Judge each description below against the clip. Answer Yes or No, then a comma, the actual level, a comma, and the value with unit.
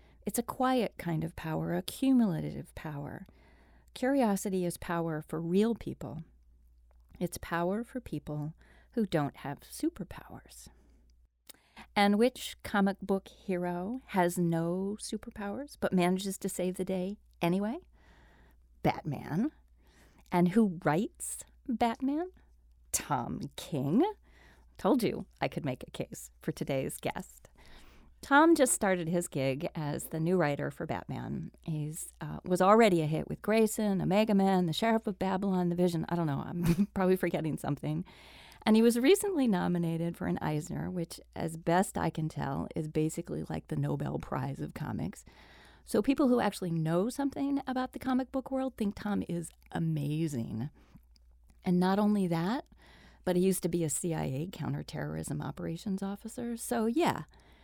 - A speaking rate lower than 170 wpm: Yes, average, 150 wpm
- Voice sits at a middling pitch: Yes, medium, 180 Hz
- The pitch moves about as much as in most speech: No, wide, 5.8 semitones